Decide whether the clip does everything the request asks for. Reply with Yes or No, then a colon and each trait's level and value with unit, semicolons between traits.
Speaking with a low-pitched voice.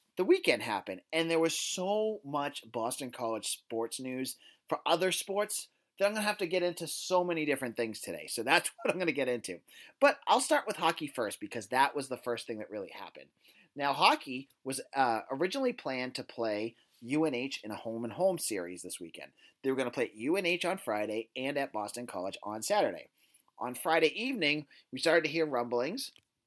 No: medium, 145 Hz